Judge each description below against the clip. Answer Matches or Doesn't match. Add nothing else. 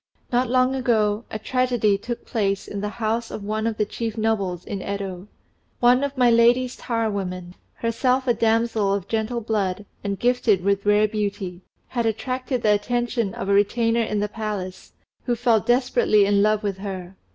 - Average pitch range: Matches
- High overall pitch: Matches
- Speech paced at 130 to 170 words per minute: Doesn't match